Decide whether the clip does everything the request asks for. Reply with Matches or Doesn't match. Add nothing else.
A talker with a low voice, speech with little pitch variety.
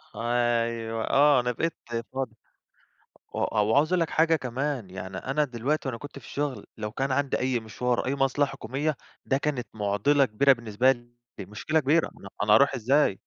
Doesn't match